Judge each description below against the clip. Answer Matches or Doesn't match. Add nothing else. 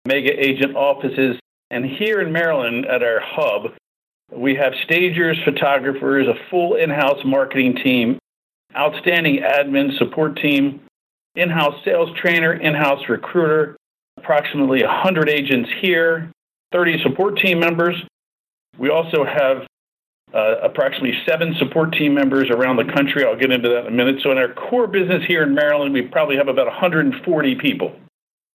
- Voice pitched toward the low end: Doesn't match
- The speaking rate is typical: Matches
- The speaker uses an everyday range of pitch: Matches